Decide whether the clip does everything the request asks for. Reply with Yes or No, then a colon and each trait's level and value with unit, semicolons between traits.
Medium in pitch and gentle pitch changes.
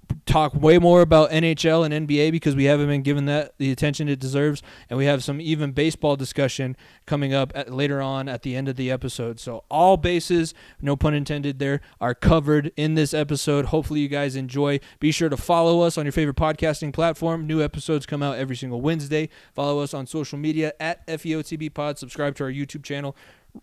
Yes: medium, 145 Hz; narrow, 2.0 semitones